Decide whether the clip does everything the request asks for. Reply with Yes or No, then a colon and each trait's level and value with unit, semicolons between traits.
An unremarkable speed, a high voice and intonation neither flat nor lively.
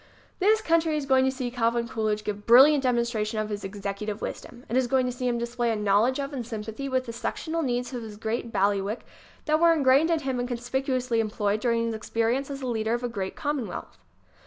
No: fast, 220 wpm; high, 240 Hz; average, 3.3 semitones